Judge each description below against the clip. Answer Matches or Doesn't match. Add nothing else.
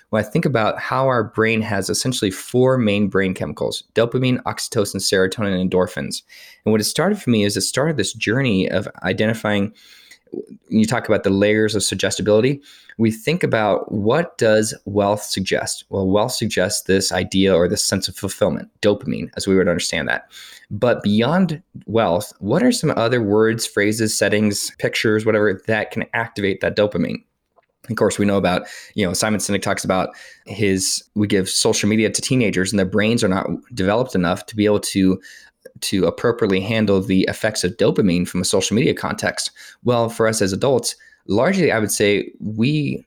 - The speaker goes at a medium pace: Matches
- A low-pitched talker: Matches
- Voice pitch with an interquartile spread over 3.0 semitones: Doesn't match